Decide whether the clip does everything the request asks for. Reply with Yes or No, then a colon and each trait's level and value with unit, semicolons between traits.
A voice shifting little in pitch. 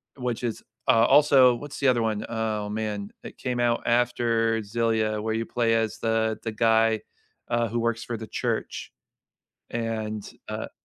Yes: narrow, 1.4 semitones